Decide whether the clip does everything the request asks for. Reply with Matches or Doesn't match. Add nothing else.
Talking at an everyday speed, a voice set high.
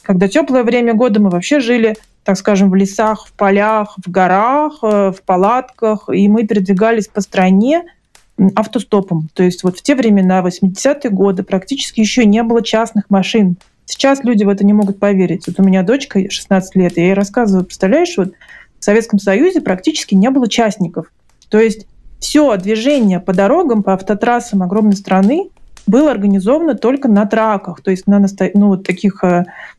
Doesn't match